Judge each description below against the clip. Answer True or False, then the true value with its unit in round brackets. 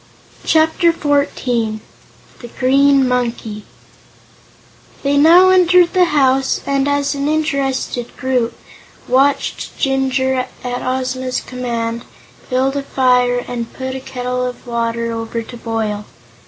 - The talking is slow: True (115 wpm)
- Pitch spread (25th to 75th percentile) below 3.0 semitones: True (2.6 semitones)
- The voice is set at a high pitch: True (260 Hz)